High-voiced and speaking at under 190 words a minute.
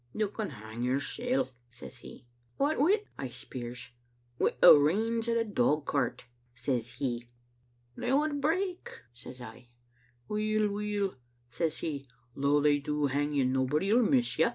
No: medium, 150 Hz; average, 155 wpm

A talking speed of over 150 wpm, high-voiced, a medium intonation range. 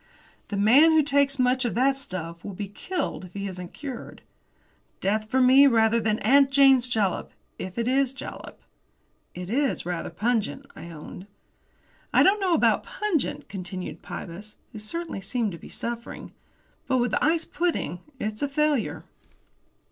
No: average, 160 wpm; high, 235 Hz; wide, 5.8 semitones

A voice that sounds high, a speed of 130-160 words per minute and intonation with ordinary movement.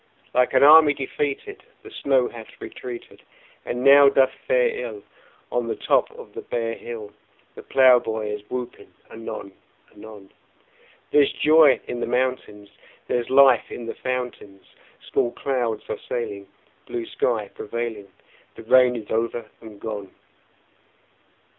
No: low, 120 Hz; slow, 135 wpm; average, 3.6 semitones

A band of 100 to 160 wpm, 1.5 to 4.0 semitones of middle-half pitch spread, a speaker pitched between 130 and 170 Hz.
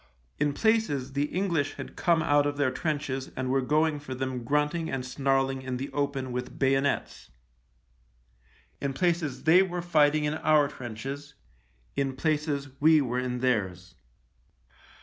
Yes: average, 150 wpm; average, 2.8 semitones; medium, 140 Hz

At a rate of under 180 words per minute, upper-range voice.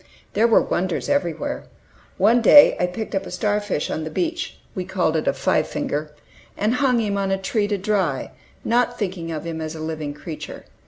No: fast, 205 wpm; high, 195 Hz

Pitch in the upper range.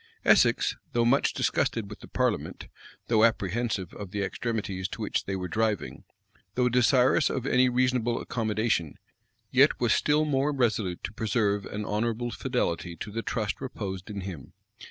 No: low, 110 Hz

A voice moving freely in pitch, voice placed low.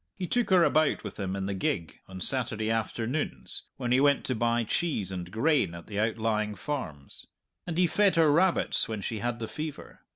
Yes: wide, 6.9 semitones; low, 115 Hz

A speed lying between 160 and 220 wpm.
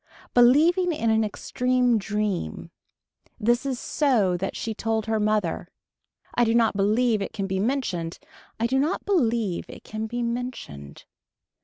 No: average, 150 wpm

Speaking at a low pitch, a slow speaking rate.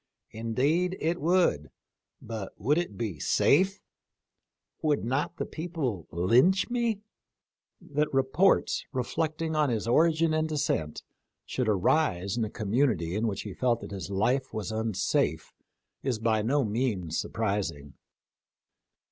Yes: low, 125 Hz; slow, 130 wpm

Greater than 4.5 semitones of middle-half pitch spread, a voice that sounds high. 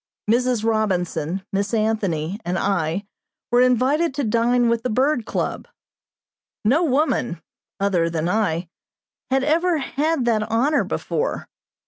Yes: average, 5.3 semitones; high, 225 Hz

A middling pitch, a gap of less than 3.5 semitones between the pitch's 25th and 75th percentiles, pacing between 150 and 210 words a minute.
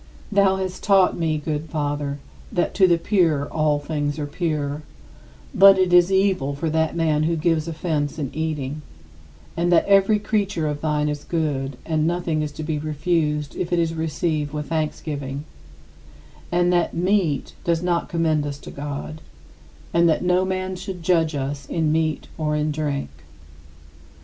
Yes: medium, 160 Hz; average, 2.9 semitones; average, 170 wpm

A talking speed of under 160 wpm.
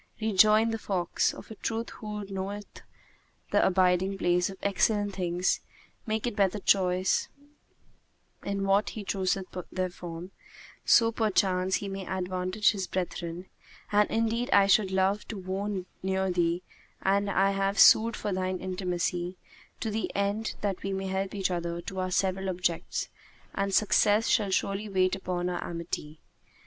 Yes: average, 150 wpm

